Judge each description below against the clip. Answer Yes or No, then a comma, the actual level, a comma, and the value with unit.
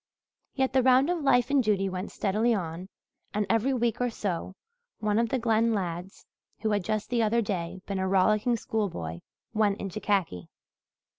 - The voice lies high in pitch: Yes, high, 210 Hz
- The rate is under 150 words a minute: No, average, 175 wpm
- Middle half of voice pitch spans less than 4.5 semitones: Yes, average, 3.7 semitones